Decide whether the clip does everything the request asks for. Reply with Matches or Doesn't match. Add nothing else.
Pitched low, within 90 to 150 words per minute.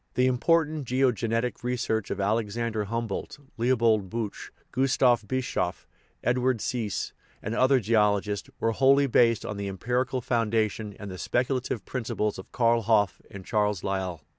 Matches